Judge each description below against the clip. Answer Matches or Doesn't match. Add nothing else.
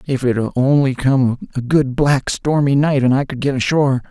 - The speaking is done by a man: Matches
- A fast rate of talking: Matches